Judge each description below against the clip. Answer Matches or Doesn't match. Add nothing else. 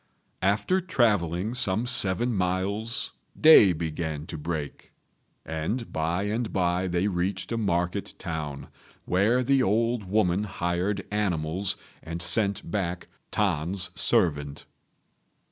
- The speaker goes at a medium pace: Doesn't match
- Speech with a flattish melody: Doesn't match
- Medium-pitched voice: Doesn't match